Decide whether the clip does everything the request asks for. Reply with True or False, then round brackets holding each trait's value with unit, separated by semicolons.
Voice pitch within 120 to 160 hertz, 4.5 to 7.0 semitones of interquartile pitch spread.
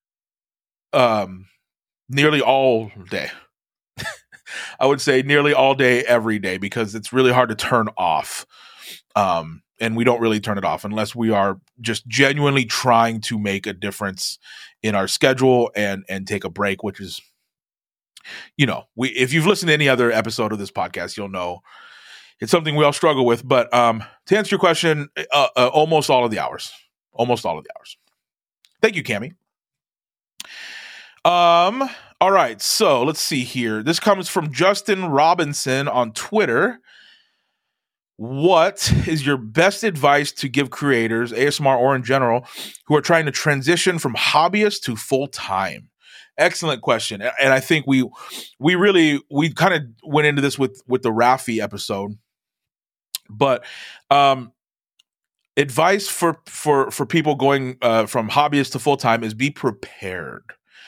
True (135 Hz; 5.1 semitones)